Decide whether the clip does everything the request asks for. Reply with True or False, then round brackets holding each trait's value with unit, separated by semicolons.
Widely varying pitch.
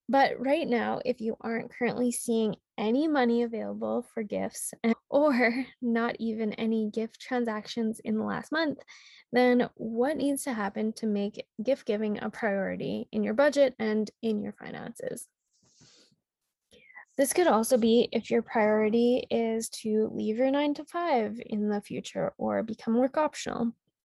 False (2.7 semitones)